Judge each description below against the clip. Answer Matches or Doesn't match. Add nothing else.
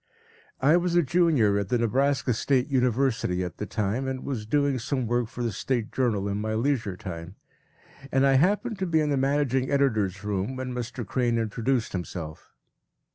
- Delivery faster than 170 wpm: Matches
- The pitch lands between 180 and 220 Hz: Doesn't match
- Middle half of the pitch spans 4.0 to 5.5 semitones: Matches